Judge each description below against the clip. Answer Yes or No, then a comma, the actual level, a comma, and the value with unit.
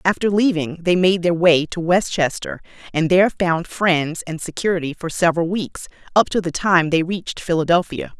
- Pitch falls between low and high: Yes, medium, 175 Hz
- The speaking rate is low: No, average, 185 wpm